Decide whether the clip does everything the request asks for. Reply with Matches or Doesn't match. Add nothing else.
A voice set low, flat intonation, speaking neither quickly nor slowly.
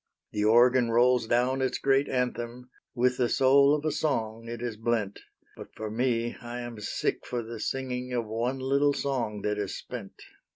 Matches